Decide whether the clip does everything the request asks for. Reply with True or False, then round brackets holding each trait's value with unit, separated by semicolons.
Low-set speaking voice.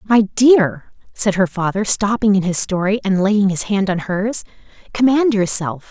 False (205 Hz)